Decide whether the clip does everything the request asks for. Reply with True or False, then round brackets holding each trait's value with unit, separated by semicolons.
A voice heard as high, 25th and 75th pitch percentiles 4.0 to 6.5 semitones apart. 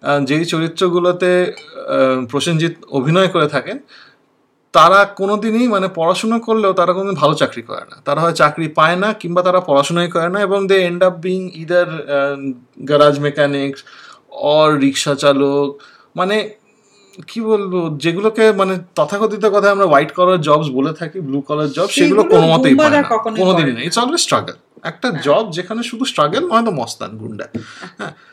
False (180 Hz; 5.5 semitones)